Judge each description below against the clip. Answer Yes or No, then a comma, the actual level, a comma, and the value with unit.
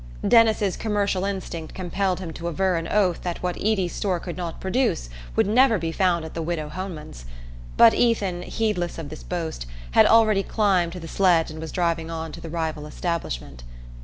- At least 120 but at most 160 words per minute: No, average, 190 wpm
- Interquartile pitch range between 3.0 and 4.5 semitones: Yes, average, 3.3 semitones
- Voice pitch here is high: No, medium, 175 Hz